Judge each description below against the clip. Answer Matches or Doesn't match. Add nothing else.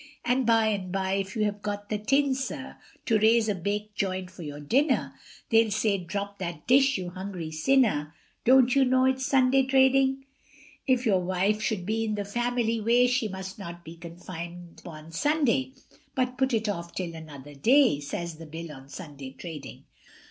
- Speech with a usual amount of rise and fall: Doesn't match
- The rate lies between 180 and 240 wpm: Matches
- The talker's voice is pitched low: Doesn't match